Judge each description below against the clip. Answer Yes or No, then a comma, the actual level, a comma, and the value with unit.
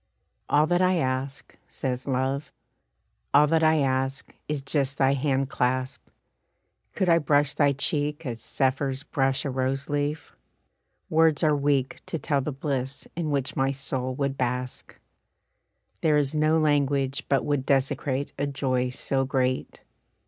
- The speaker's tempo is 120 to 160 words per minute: Yes, average, 150 wpm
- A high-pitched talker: No, medium, 140 Hz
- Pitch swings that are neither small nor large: No, narrow, 1.9 semitones